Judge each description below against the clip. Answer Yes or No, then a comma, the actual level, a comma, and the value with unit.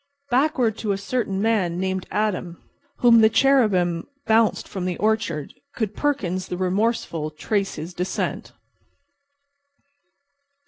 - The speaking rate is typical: No, slow, 120 wpm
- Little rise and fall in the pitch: No, average, 3.9 semitones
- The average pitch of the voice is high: Yes, high, 200 Hz